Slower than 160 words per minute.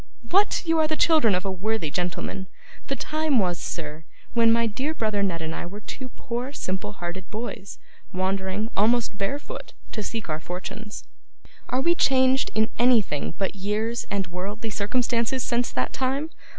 No: average, 165 wpm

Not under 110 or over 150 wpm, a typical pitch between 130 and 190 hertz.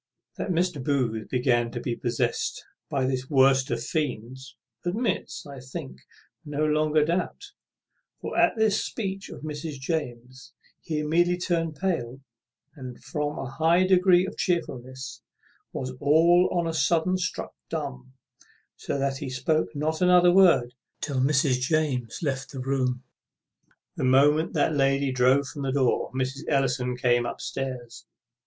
Yes: average, 145 wpm; medium, 140 Hz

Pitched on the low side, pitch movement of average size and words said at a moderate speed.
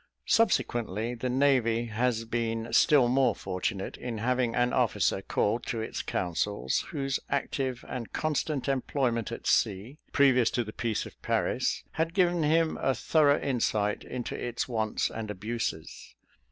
Yes: low, 120 Hz; average, 3.4 semitones; average, 145 wpm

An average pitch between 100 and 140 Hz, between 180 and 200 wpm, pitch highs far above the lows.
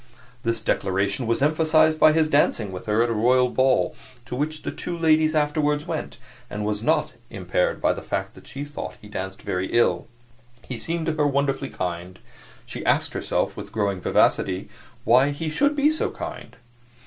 Yes: low, 135 Hz; average, 185 wpm; wide, 6.7 semitones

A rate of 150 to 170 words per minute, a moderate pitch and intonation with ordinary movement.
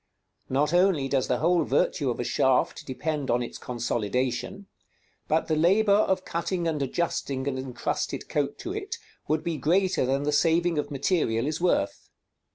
Yes: average, 165 wpm; medium, 150 Hz; average, 4.9 semitones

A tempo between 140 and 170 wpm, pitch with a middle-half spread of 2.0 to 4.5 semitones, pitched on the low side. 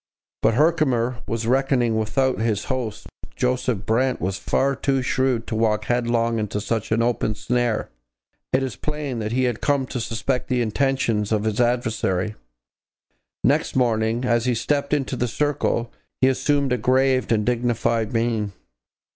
Yes: average, 155 wpm; average, 2.8 semitones; low, 120 Hz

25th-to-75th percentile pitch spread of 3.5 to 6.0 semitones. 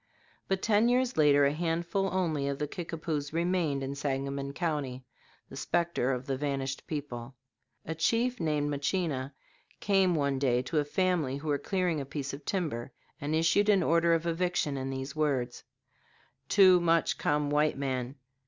Yes: average, 3.9 semitones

